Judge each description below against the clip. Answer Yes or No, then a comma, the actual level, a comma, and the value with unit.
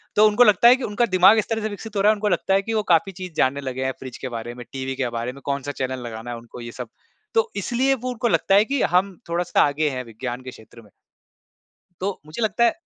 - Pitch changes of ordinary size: No, wide, 8.7 semitones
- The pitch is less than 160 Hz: No, medium, 180 Hz